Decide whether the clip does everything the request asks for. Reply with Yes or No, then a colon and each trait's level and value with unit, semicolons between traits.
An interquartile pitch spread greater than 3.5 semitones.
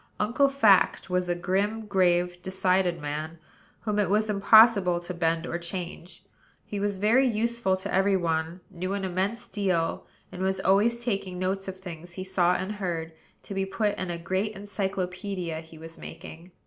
No: narrow, 2.6 semitones